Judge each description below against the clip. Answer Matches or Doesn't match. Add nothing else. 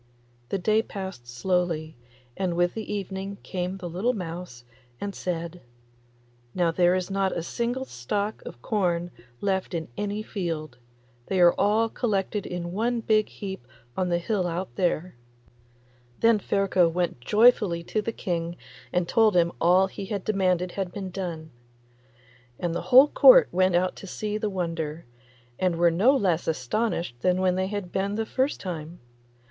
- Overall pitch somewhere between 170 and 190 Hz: Matches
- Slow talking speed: Doesn't match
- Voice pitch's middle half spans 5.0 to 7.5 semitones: Doesn't match